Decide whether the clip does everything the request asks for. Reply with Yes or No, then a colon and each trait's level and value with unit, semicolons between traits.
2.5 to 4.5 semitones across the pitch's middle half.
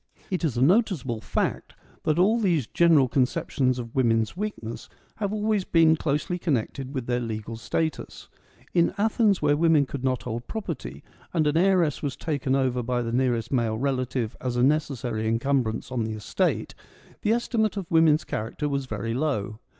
No: wide, 5.6 semitones